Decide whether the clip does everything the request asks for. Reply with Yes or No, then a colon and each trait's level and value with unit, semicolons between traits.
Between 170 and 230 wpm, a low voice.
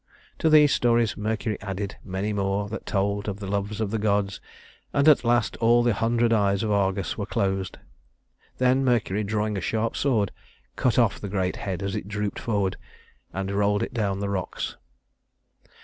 Yes: average, 180 wpm; low, 105 Hz